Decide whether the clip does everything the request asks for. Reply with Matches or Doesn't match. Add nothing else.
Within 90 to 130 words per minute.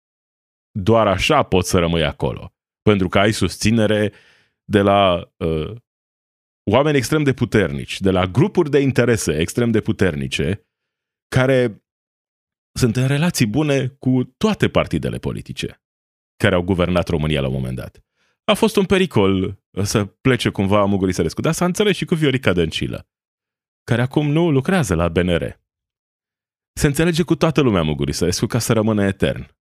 Doesn't match